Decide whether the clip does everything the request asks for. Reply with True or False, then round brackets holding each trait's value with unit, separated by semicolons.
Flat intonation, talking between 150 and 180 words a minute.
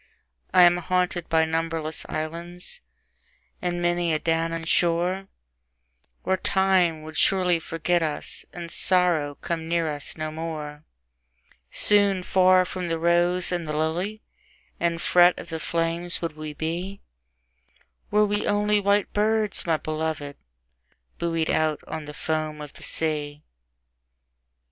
False (2.3 semitones; 135 wpm)